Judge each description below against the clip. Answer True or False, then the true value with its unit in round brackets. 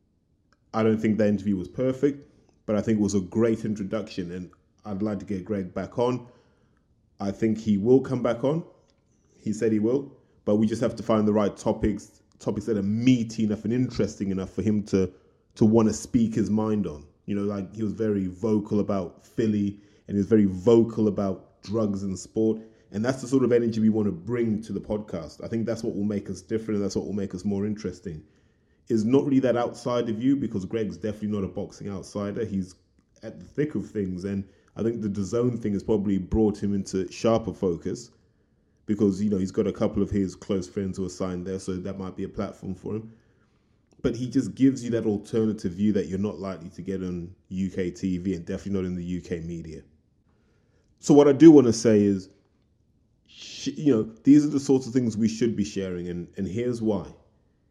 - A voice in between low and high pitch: False (105 Hz)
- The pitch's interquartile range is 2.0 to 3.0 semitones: True (2.7 semitones)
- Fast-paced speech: True (220 wpm)